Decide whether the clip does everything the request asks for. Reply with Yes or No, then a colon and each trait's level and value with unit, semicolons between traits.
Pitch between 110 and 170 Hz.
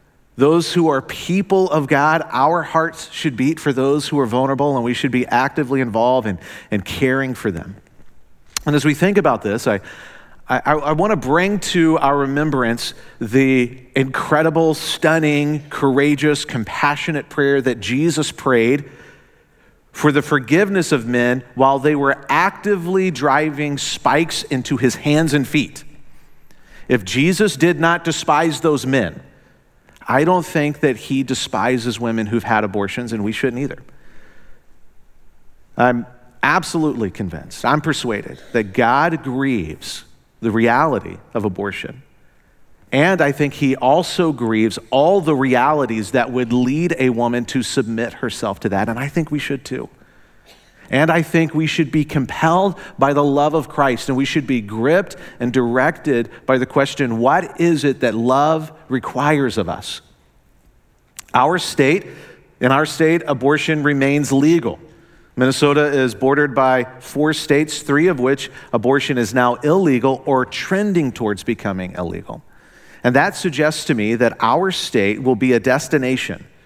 Yes: medium, 140 Hz